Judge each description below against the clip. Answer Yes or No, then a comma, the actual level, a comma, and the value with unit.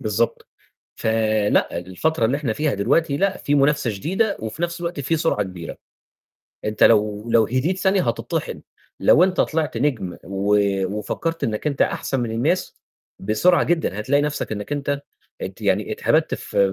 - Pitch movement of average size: No, wide, 7.3 semitones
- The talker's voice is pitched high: No, medium, 140 Hz